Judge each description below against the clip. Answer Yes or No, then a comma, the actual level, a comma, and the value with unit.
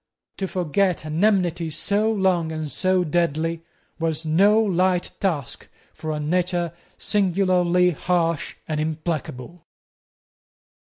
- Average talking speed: No, slow, 110 wpm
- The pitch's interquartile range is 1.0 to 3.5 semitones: Yes, average, 2.8 semitones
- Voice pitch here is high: No, medium, 175 Hz